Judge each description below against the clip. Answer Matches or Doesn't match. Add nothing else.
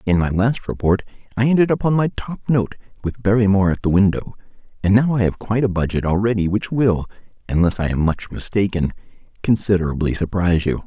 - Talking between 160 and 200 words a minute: Matches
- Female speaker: Doesn't match